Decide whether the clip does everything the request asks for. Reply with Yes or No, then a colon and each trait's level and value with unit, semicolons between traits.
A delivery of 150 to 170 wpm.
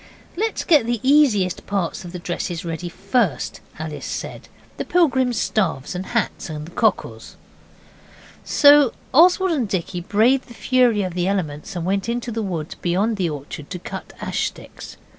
Yes: average, 165 wpm